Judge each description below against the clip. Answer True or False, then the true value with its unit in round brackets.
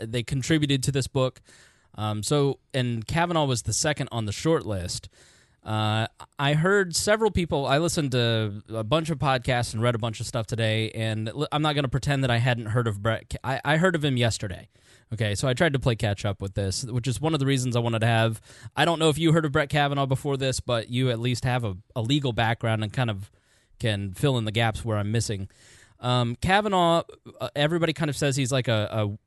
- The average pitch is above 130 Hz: False (125 Hz)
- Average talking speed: False (235 wpm)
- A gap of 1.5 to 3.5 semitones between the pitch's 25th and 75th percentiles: False (4.3 semitones)